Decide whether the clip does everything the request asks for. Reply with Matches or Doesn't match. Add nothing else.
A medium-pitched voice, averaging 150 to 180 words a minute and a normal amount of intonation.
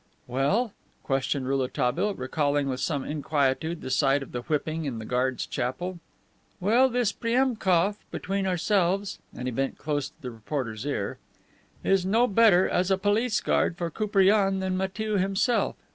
Doesn't match